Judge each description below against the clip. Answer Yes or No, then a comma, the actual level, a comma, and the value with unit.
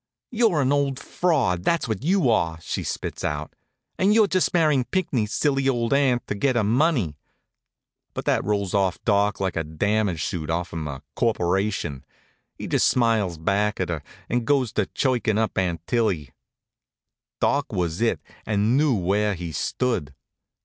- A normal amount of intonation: No, wide, 7.0 semitones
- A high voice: No, low, 105 Hz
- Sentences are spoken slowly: No, average, 165 wpm